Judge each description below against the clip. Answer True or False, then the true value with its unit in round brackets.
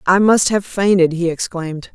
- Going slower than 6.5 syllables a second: True (5.0 syllables/s)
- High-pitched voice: False (180 Hz)